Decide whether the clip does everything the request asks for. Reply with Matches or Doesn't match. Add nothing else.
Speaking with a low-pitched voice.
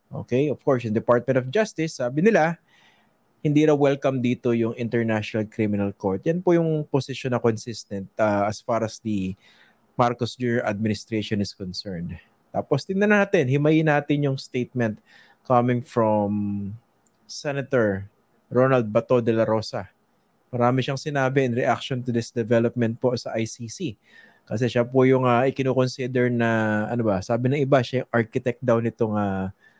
Matches